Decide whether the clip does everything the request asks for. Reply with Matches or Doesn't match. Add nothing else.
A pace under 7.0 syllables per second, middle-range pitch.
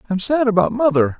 Doesn't match